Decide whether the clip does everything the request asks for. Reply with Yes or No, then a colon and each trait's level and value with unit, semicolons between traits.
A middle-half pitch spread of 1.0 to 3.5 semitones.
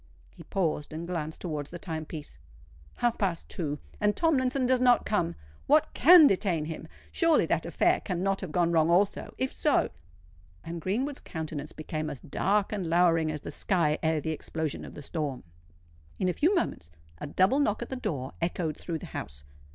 No: average, 5.2 semitones